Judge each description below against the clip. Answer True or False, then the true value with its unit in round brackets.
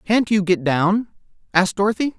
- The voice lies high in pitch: True (195 Hz)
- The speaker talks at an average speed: True (165 wpm)